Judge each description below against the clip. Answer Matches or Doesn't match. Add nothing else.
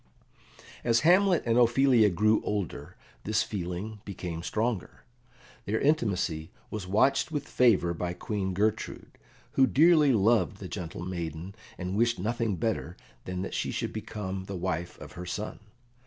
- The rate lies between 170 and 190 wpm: Doesn't match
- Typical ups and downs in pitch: Matches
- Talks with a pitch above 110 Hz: Doesn't match